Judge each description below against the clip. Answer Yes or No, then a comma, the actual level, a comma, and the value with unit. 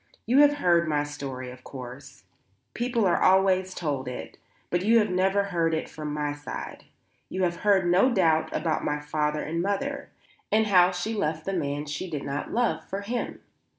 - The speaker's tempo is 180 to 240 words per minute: Yes, average, 185 wpm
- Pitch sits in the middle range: Yes, medium, 175 Hz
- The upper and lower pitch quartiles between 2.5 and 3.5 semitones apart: No, average, 5.1 semitones